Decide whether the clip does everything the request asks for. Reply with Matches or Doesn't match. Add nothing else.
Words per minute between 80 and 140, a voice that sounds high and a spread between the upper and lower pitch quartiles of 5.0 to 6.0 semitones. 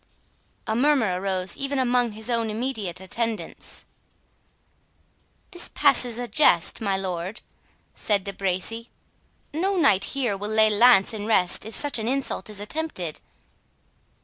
Doesn't match